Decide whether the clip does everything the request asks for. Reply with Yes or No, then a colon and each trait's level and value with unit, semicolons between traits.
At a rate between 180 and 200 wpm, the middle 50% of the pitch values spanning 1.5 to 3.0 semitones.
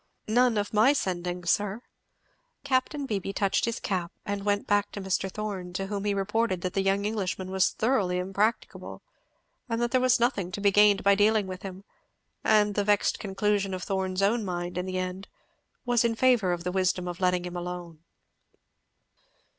Yes: average, 185 wpm; narrow, 2.5 semitones